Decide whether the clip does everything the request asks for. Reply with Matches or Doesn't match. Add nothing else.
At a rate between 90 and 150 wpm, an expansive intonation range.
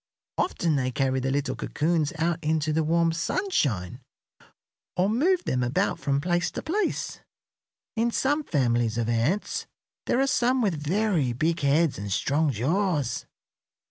Matches